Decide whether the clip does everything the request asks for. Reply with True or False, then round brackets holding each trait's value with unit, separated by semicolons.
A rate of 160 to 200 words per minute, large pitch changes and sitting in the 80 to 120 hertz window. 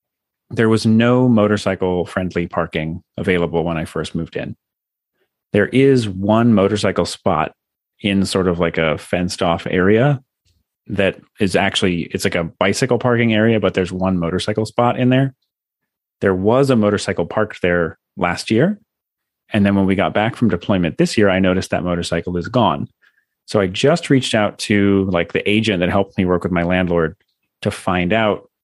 False (175 wpm; 3.7 semitones; 100 Hz)